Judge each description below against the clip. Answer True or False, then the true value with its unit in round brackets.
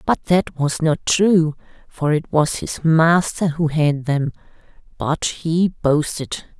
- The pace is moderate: True (145 wpm)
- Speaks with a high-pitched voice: False (155 Hz)